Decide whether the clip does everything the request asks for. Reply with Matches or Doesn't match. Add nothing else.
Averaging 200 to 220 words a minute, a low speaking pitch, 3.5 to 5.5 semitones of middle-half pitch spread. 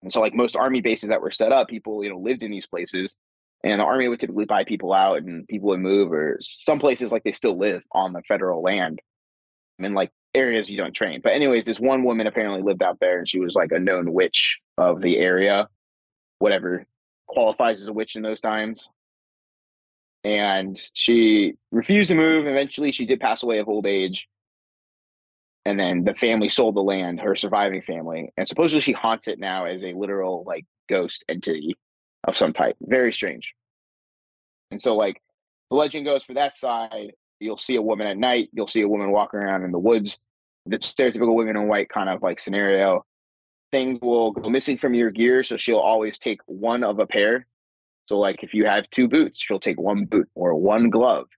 Matches